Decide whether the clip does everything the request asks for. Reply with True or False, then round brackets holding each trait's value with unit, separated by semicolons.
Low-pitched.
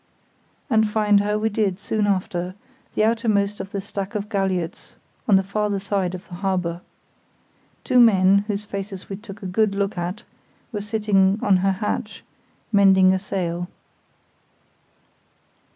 False (200 Hz)